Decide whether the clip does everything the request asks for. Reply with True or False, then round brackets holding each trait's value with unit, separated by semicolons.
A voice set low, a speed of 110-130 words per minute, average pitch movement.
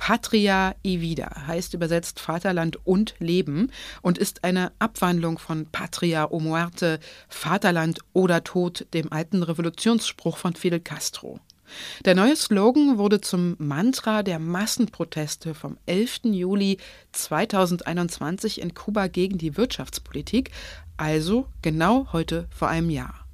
False (180 Hz; 125 wpm; 3.9 semitones)